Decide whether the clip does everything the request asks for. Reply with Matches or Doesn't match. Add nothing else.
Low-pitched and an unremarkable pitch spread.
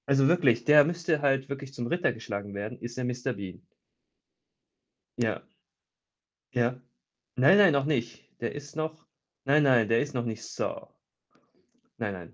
Matches